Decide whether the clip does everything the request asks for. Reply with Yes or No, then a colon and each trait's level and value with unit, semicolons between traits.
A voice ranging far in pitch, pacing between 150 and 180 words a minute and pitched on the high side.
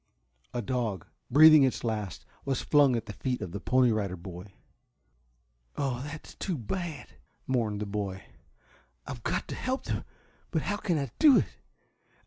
No: wide, 5.8 semitones; average, 160 wpm; low, 125 Hz